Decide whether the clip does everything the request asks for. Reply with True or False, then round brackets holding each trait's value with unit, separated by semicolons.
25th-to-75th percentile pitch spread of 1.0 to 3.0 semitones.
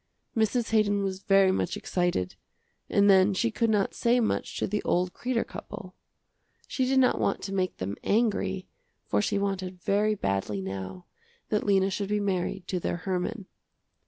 True (2.6 semitones)